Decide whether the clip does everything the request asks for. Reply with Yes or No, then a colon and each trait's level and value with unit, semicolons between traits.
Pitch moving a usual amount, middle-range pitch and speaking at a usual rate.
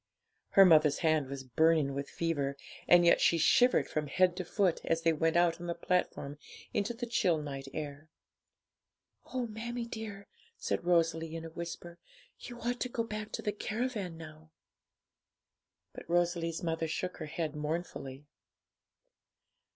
Yes: average, 4.1 semitones; medium, 170 Hz; average, 155 wpm